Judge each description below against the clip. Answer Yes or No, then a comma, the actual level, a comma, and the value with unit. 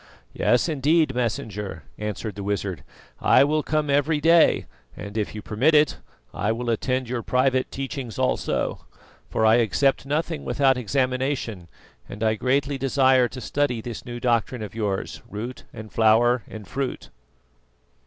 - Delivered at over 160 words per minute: No, average, 150 wpm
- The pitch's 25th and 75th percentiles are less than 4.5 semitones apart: Yes, average, 4.0 semitones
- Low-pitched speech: Yes, low, 125 Hz